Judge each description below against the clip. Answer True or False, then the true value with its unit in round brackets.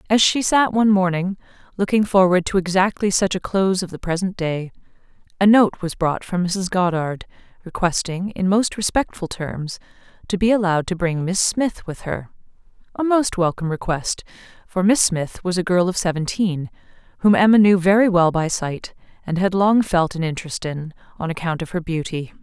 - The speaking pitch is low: False (185 Hz)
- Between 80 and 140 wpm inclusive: False (180 wpm)